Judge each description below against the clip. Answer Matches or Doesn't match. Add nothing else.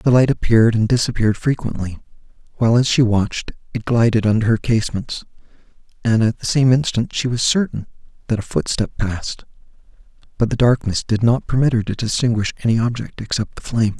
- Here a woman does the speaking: Doesn't match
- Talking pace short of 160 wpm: Doesn't match